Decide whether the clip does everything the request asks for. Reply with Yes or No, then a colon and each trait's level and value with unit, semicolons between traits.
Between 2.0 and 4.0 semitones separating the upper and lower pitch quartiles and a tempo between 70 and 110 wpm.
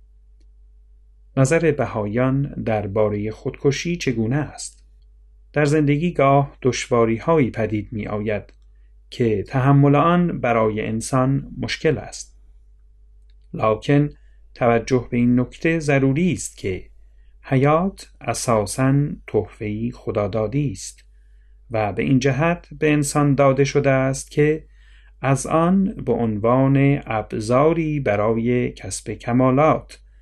No: wide, 5.6 semitones; slow, 105 wpm